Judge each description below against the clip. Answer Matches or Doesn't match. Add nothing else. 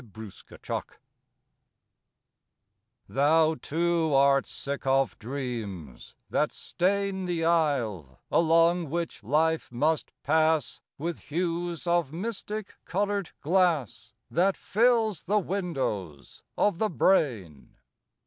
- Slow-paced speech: Matches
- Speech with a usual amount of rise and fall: Matches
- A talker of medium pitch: Matches